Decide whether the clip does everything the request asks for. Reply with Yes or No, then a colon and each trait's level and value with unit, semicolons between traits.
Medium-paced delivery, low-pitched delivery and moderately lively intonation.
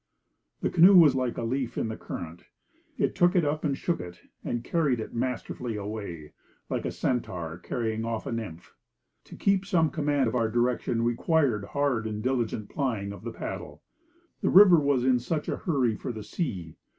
Yes: average, 185 wpm; low, 120 Hz; average, 4.9 semitones